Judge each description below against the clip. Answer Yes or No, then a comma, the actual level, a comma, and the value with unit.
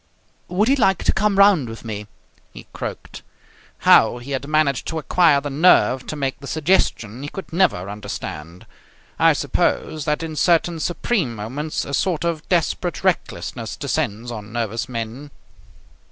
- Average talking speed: Yes, average, 155 wpm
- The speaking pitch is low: No, medium, 145 Hz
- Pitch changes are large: Yes, wide, 6.6 semitones